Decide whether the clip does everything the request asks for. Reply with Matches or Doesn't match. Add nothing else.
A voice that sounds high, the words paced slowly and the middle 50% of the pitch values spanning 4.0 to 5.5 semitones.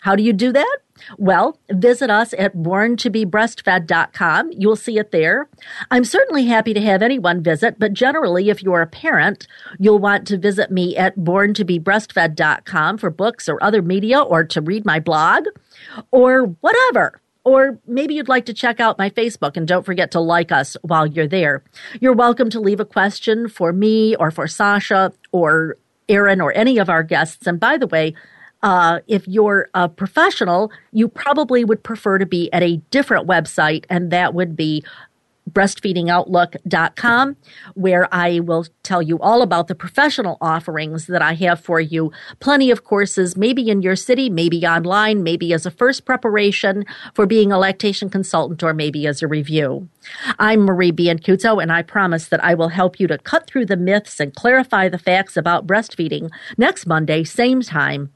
Doesn't match